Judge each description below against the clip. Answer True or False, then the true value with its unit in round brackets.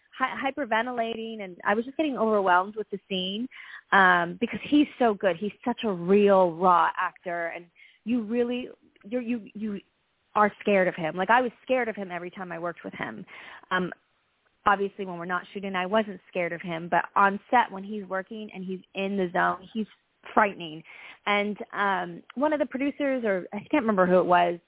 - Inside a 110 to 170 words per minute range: False (195 wpm)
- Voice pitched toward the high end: True (200 Hz)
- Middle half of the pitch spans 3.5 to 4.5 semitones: True (4.2 semitones)